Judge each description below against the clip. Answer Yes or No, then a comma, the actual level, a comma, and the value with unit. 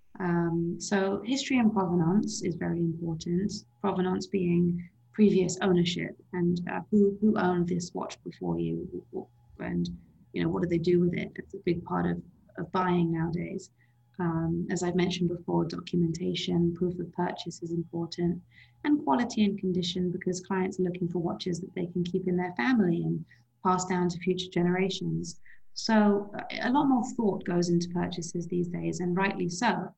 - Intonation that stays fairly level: Yes, narrow, 1.7 semitones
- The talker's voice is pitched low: No, medium, 180 Hz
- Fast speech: No, average, 170 wpm